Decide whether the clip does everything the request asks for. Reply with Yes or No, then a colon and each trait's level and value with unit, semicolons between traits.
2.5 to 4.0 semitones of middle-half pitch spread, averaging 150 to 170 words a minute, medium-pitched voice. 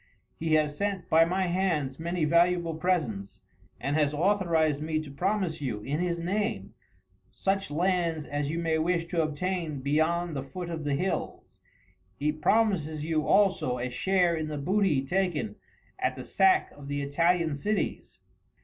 Yes: average, 3.6 semitones; average, 160 wpm; medium, 165 Hz